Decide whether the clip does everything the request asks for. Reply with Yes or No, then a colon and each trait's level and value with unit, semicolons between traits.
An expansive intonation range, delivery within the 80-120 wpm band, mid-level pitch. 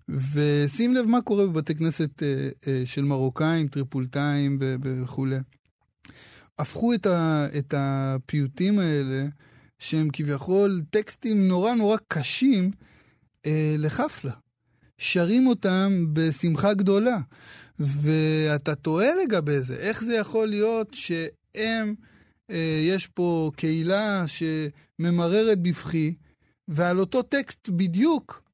Yes: wide, 5.9 semitones; average, 105 wpm; medium, 160 Hz